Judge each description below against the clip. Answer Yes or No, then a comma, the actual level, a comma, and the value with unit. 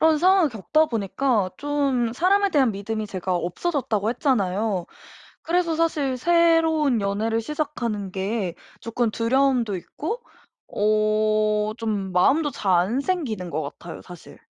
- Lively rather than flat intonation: Yes, wide, 6.8 semitones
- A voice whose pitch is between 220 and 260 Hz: Yes, high, 230 Hz